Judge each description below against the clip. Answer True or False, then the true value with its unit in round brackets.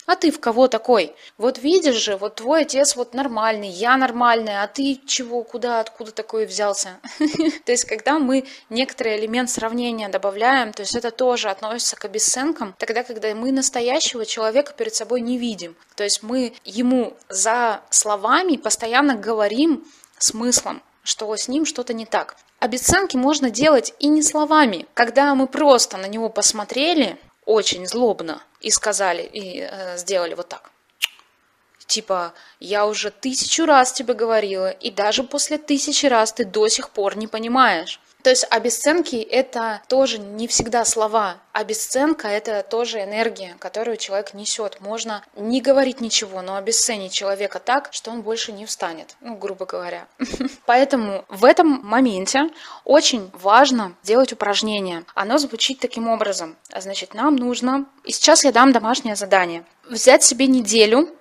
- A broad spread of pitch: False (4.0 semitones)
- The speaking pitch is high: True (235 Hz)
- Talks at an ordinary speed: True (150 wpm)